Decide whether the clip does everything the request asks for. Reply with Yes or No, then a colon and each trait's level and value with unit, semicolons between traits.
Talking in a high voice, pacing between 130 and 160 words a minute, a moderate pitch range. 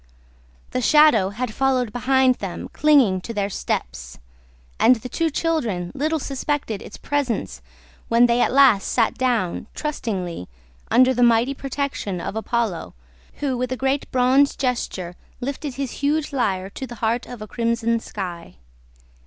Yes: high, 245 Hz; average, 150 wpm; average, 4.4 semitones